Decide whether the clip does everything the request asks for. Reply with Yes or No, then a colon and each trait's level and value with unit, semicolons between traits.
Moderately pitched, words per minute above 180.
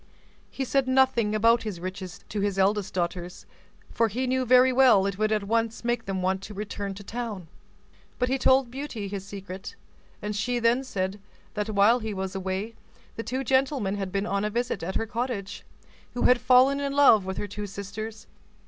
No: high, 215 Hz; average, 195 wpm